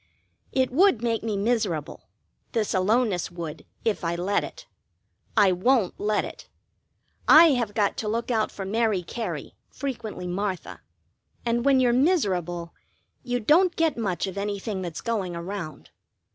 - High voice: Yes, high, 210 Hz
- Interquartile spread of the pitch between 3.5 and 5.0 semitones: Yes, average, 4.6 semitones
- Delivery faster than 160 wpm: No, average, 145 wpm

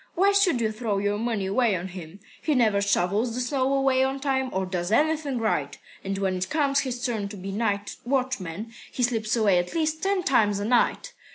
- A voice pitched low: No, high, 225 Hz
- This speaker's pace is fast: Yes, fast, 210 wpm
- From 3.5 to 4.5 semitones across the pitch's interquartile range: No, average, 5.1 semitones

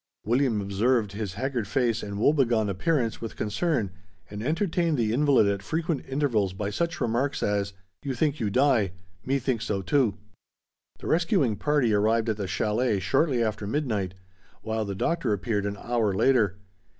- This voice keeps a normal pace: Yes, average, 165 wpm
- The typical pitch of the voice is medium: No, low, 115 Hz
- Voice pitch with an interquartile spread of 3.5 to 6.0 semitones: Yes, average, 5.1 semitones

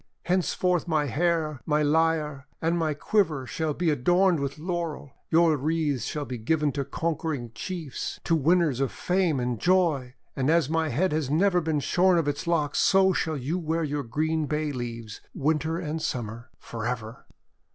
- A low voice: No, medium, 155 Hz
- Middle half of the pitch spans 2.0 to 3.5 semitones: Yes, average, 3.2 semitones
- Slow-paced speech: No, average, 175 wpm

